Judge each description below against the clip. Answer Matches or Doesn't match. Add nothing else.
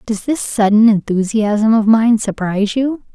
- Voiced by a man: Doesn't match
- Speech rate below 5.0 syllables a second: Matches